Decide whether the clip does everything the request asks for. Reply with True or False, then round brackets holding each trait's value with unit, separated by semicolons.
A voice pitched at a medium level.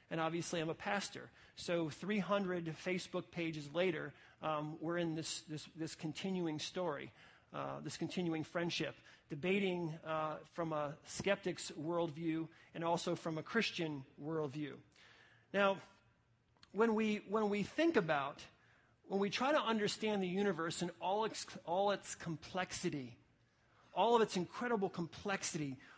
True (170 Hz)